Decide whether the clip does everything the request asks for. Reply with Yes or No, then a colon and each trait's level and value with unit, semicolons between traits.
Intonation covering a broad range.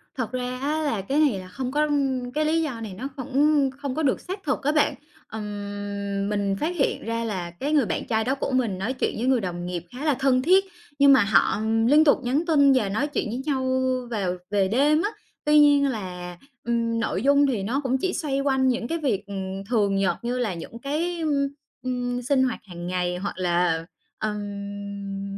Yes: wide, 5.8 semitones